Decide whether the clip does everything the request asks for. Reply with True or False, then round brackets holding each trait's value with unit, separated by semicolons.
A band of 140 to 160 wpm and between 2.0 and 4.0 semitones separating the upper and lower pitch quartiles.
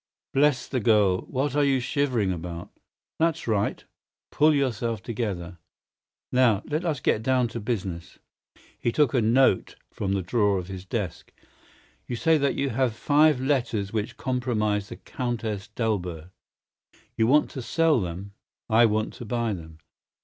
False (155 wpm; 4.7 semitones)